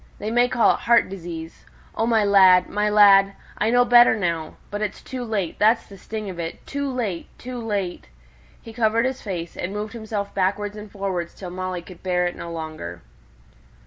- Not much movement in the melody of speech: No, average, 3.9 semitones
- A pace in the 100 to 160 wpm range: No, average, 195 wpm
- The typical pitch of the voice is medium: No, high, 205 Hz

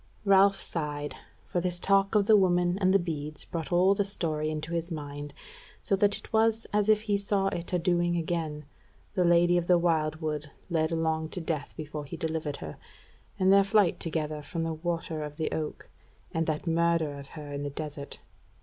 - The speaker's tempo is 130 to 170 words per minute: No, average, 195 wpm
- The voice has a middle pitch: Yes, medium, 165 Hz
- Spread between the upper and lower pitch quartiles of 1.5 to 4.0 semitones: Yes, average, 3.3 semitones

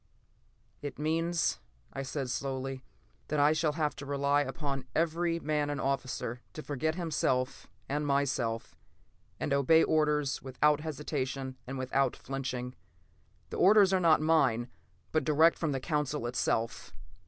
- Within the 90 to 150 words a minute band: Yes, average, 140 wpm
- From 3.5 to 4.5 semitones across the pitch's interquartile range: No, average, 2.8 semitones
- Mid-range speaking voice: Yes, medium, 145 Hz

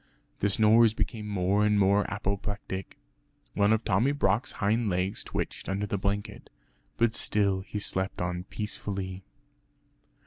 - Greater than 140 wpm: No, slow, 135 wpm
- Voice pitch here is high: No, low, 100 Hz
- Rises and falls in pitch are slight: Yes, narrow, 1.9 semitones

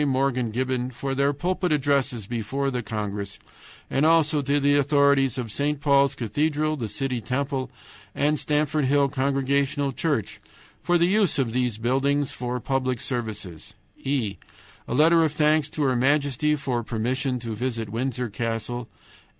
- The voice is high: No, low, 135 Hz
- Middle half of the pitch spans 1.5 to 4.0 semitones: Yes, average, 3.0 semitones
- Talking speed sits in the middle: Yes, average, 150 wpm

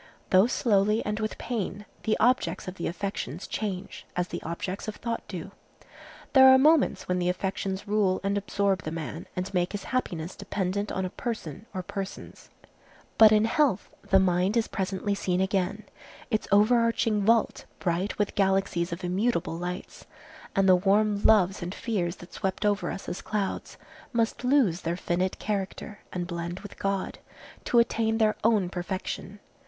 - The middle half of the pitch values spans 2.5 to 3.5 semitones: Yes, average, 2.9 semitones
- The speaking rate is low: No, average, 165 wpm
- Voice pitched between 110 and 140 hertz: No, high, 195 Hz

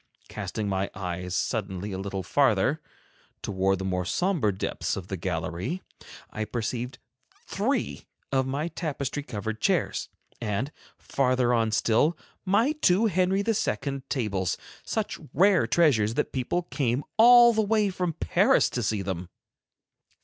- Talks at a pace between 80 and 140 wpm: Yes, slow, 135 wpm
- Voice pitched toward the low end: Yes, low, 120 Hz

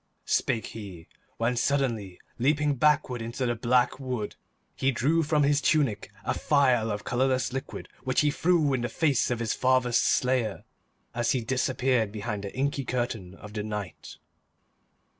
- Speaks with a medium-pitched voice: No, low, 125 Hz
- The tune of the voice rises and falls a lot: No, average, 3.4 semitones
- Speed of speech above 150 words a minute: Yes, average, 160 wpm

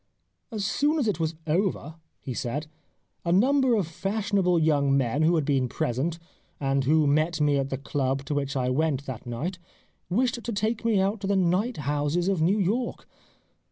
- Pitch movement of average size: No, wide, 6.1 semitones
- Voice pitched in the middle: Yes, medium, 160 Hz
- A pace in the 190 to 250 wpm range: Yes, average, 195 wpm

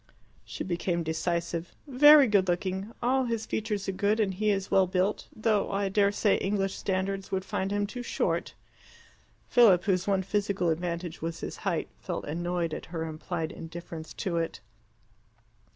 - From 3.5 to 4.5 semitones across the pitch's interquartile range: No, average, 3.0 semitones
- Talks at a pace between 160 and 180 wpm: Yes, average, 165 wpm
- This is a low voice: No, high, 190 Hz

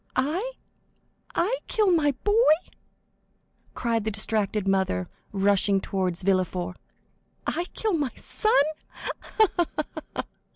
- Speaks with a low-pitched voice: No, high, 220 Hz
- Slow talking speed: Yes, slow, 100 wpm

